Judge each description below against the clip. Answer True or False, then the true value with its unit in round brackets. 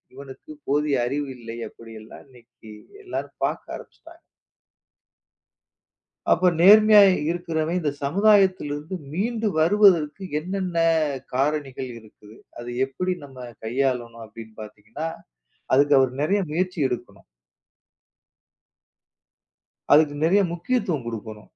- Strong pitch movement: True (7.1 semitones)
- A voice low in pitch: False (150 Hz)